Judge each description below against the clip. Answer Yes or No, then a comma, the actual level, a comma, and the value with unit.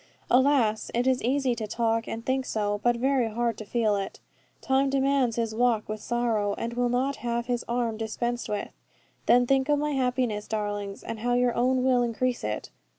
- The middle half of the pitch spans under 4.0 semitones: Yes, narrow, 2.6 semitones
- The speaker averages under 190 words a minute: No, average, 195 wpm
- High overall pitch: Yes, high, 240 Hz